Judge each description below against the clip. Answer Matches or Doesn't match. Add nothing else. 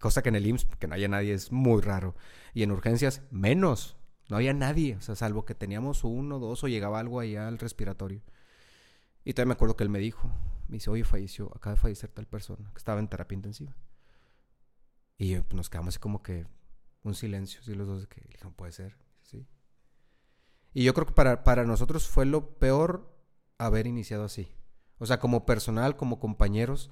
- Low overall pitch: Matches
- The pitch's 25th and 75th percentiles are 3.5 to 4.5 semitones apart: Matches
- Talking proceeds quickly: Matches